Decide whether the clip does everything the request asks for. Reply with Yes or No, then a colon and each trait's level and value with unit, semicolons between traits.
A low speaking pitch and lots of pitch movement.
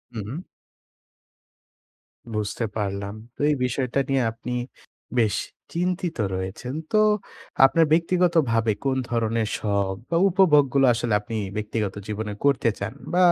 Yes: low, 120 Hz; wide, 6.4 semitones